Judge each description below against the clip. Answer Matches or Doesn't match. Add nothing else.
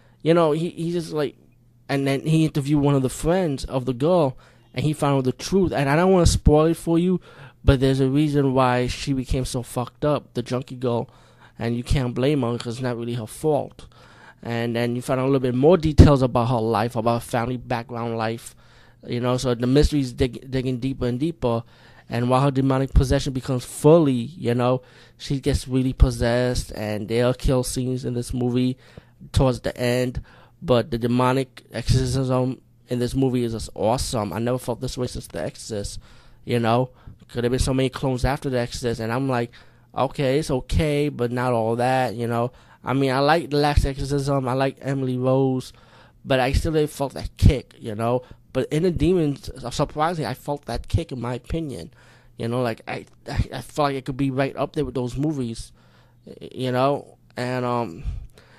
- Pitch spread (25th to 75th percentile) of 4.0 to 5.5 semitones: Doesn't match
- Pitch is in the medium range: Doesn't match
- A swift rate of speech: Matches